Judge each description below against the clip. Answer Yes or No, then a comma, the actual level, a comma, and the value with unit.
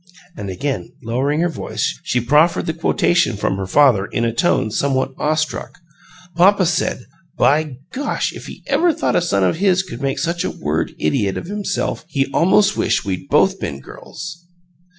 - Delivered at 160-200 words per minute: Yes, average, 180 wpm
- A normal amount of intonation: No, wide, 6.7 semitones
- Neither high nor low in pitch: Yes, medium, 150 Hz